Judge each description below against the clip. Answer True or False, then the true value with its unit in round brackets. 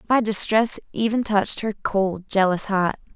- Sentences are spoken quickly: False (150 wpm)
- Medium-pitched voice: False (205 Hz)